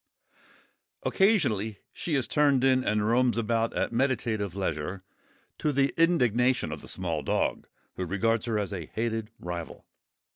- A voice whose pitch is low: Yes, low, 115 Hz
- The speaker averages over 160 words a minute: No, average, 145 wpm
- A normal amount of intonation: Yes, average, 4.8 semitones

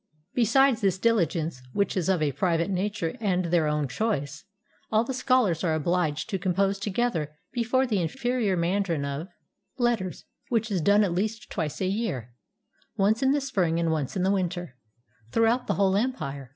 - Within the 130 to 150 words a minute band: No, average, 175 wpm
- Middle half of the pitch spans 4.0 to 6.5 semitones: Yes, average, 5.3 semitones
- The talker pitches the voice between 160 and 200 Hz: Yes, high, 190 Hz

